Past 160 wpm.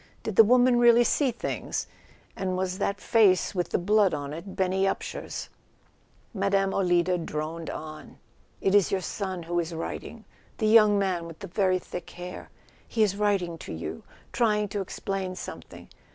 Yes: average, 170 wpm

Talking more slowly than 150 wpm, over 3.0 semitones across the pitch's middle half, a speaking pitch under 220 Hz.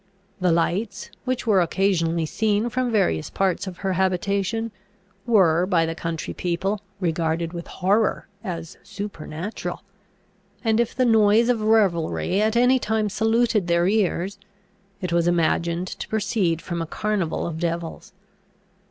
Yes: average, 140 wpm; average, 4.2 semitones; high, 190 Hz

